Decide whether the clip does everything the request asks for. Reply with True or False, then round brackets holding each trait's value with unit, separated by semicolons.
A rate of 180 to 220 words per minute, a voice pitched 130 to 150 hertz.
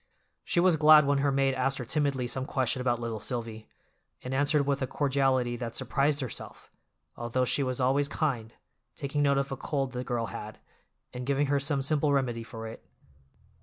True (190 wpm; 135 Hz)